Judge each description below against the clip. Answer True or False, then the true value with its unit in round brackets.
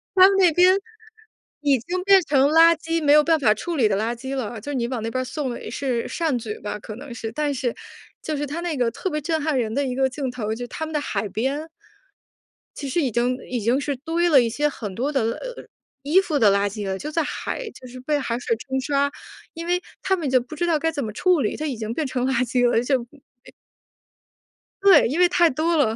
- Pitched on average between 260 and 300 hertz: True (275 Hz)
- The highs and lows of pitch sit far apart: False (4.9 semitones)